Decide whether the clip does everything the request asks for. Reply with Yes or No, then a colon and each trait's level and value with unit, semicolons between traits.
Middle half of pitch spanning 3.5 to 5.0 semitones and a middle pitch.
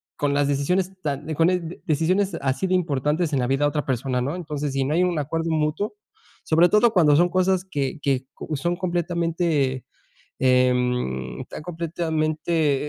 Yes: average, 4.1 semitones; medium, 155 Hz